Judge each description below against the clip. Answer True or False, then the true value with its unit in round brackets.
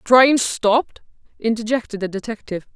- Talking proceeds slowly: True (130 wpm)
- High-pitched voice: True (225 Hz)